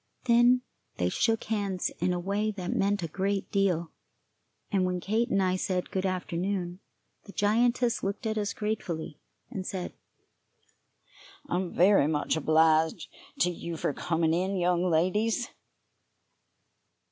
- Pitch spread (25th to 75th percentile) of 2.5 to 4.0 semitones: Yes, average, 3.0 semitones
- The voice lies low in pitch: No, medium, 185 Hz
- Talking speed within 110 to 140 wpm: Yes, slow, 135 wpm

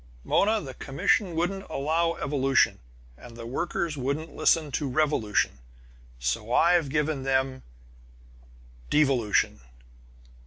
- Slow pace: Yes, slow, 105 wpm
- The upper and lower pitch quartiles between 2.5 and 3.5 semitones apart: No, average, 4.1 semitones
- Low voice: No, medium, 145 Hz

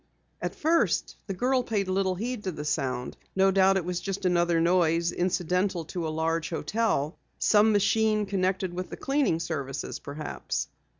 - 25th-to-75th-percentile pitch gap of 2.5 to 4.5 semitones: Yes, average, 3.6 semitones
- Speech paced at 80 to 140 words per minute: No, average, 165 wpm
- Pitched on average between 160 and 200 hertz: Yes, medium, 185 Hz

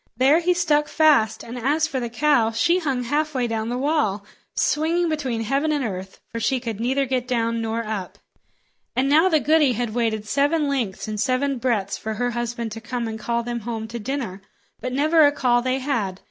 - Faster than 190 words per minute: Yes, fast, 205 wpm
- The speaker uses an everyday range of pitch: Yes, average, 4.2 semitones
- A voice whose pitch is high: Yes, high, 245 Hz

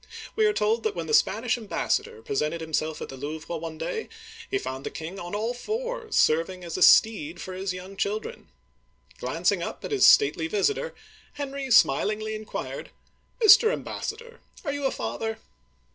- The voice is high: Yes, high, 215 Hz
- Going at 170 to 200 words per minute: Yes, average, 175 wpm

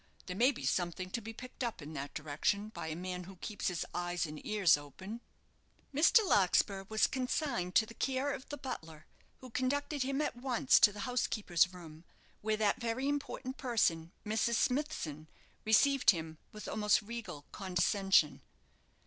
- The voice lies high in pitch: Yes, high, 210 Hz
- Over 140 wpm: Yes, average, 165 wpm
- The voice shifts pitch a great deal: Yes, wide, 6.3 semitones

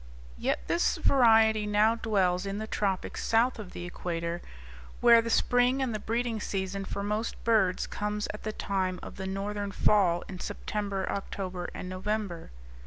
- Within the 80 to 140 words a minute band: No, average, 165 wpm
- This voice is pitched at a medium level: No, high, 205 Hz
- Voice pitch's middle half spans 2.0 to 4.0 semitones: Yes, average, 2.8 semitones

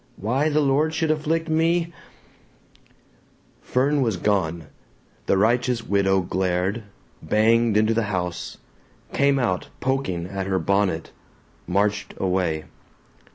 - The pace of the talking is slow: Yes, slow, 115 wpm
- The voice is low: Yes, low, 105 Hz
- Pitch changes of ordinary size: No, wide, 6.3 semitones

